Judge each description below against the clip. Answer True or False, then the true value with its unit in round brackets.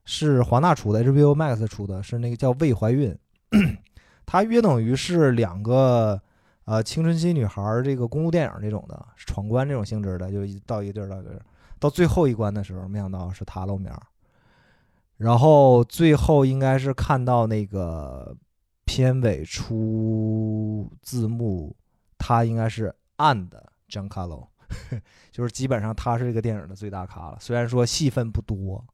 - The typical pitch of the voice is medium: False (110 Hz)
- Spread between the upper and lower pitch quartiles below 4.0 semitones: False (4.7 semitones)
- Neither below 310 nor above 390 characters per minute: False (260 characters per minute)